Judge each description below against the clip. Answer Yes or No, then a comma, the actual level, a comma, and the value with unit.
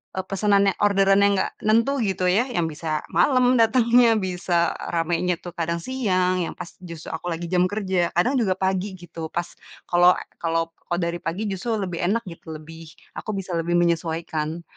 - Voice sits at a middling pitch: Yes, medium, 180 Hz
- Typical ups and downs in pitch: Yes, average, 3.2 semitones